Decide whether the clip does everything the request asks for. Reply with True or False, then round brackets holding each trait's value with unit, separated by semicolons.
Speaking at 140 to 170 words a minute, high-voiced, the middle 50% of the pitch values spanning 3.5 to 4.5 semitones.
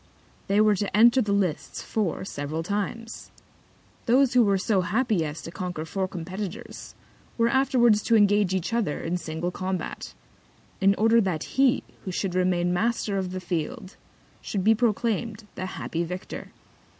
True (160 wpm; 195 Hz; 3.8 semitones)